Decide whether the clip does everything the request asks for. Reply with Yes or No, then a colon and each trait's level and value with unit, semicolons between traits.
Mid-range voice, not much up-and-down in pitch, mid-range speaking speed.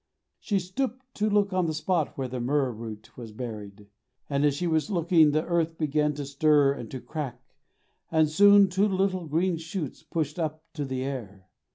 No: medium, 155 Hz; average, 5.1 semitones; average, 190 wpm